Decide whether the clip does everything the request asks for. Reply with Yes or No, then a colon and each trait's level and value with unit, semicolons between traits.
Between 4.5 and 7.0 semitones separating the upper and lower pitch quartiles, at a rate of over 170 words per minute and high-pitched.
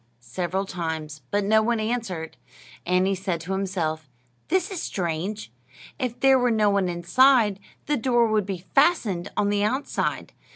No: average, 5.1 semitones; average, 160 wpm; high, 200 Hz